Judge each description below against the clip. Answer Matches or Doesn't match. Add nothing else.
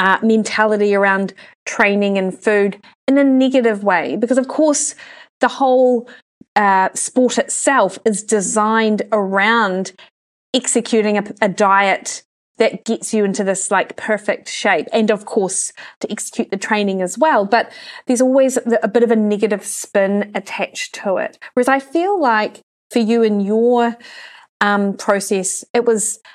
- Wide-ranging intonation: Doesn't match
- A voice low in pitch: Doesn't match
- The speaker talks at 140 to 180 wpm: Matches